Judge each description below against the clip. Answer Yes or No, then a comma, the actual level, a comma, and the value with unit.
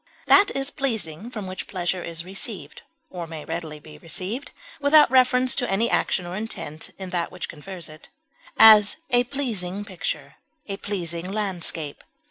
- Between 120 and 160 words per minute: Yes, average, 155 wpm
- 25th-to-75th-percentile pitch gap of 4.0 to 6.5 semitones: Yes, average, 5.3 semitones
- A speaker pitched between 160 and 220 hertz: Yes, high, 190 Hz